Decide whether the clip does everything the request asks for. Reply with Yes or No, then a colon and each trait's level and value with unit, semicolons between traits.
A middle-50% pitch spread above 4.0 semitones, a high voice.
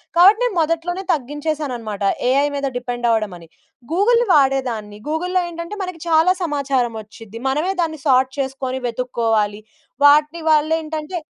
Yes: wide, 5.4 semitones; very high, 285 Hz